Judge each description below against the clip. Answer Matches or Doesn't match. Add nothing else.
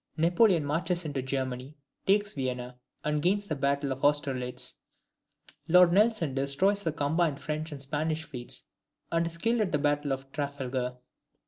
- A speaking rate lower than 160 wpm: Matches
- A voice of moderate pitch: Matches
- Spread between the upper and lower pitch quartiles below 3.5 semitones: Doesn't match